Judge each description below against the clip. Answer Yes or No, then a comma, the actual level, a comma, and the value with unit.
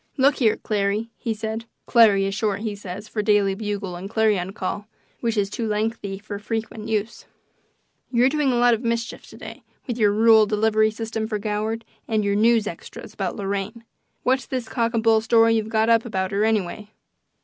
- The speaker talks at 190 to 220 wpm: Yes, average, 195 wpm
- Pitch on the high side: Yes, high, 220 Hz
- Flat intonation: Yes, narrow, 1.9 semitones